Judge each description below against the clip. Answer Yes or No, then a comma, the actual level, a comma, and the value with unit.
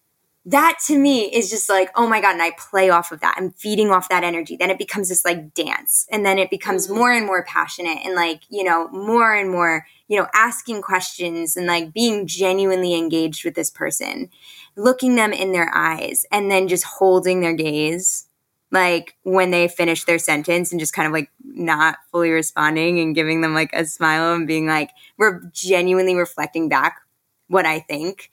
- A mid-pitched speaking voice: Yes, medium, 180 Hz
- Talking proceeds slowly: No, average, 200 wpm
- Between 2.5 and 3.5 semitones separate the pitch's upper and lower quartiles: Yes, average, 2.9 semitones